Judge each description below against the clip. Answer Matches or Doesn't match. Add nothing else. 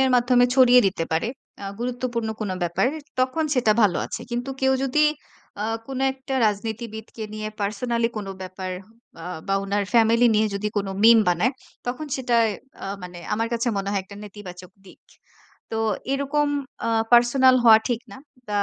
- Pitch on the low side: Doesn't match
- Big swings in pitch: Doesn't match